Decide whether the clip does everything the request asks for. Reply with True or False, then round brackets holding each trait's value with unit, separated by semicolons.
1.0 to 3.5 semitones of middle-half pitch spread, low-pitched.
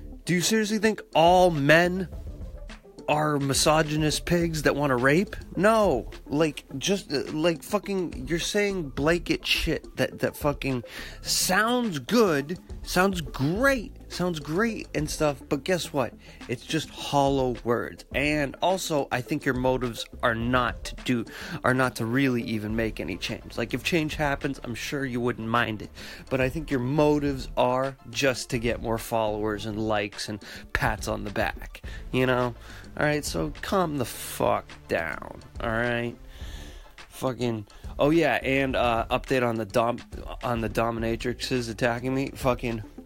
False (5.0 semitones; 130 Hz)